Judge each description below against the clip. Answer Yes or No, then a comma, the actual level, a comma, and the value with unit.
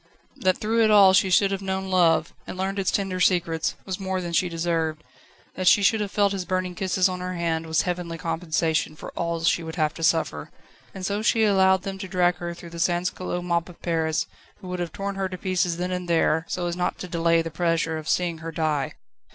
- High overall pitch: No, medium, 180 Hz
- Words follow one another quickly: Yes, fast, 235 wpm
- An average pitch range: No, narrow, 2.3 semitones